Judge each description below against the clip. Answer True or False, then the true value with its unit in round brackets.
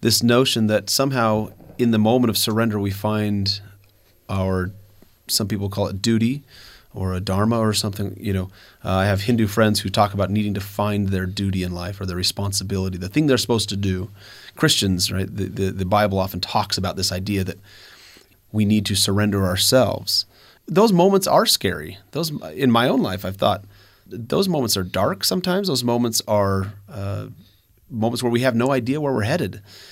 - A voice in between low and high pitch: False (100 Hz)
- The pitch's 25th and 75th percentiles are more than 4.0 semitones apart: False (3.0 semitones)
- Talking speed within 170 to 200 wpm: True (180 wpm)